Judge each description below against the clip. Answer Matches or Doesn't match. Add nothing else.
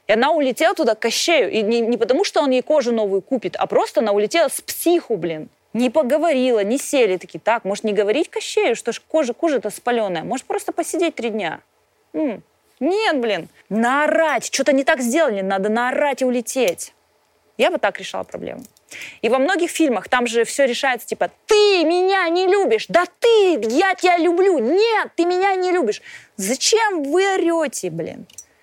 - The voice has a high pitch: Matches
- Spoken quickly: Matches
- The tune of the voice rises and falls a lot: Matches